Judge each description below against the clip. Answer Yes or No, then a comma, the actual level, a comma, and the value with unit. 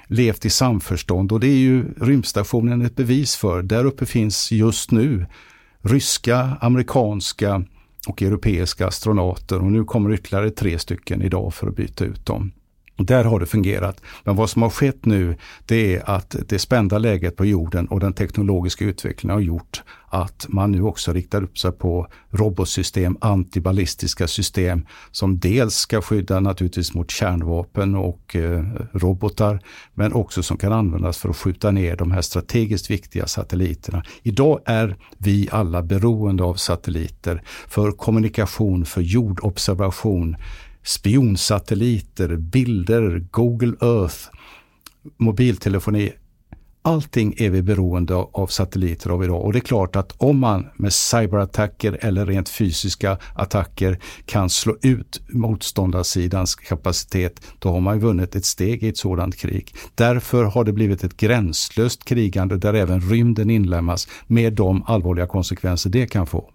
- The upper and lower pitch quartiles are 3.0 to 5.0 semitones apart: Yes, average, 3.6 semitones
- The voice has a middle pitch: No, low, 100 Hz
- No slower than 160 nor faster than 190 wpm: No, average, 145 wpm